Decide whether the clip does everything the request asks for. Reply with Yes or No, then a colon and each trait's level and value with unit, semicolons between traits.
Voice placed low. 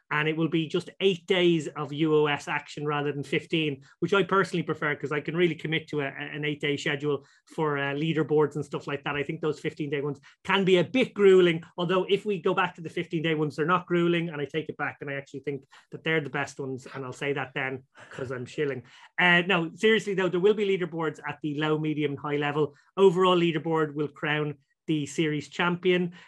No: medium, 155 Hz